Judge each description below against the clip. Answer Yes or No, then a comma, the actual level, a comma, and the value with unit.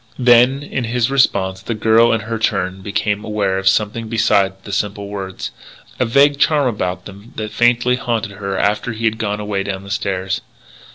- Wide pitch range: No, average, 3.1 semitones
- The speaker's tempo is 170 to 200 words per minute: Yes, average, 185 wpm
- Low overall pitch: Yes, low, 105 Hz